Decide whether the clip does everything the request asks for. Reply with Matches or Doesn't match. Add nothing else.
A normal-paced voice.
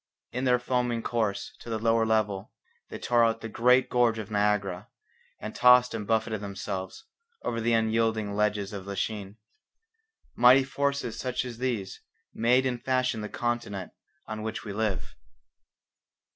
Matches